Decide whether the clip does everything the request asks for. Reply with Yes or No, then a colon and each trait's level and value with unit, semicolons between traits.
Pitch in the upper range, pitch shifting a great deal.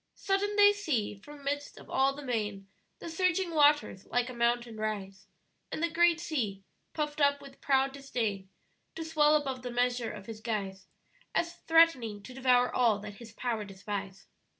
Yes: very high, 250 Hz; wide, 6.0 semitones